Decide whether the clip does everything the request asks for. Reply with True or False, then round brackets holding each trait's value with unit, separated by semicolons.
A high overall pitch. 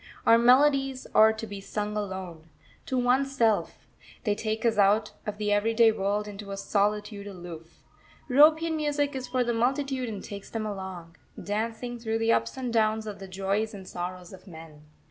True (215 Hz)